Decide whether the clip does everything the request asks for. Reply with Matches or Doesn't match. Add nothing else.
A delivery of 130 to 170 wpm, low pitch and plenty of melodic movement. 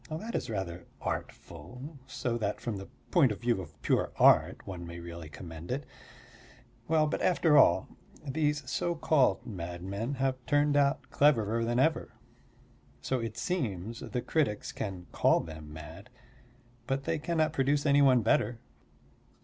Matches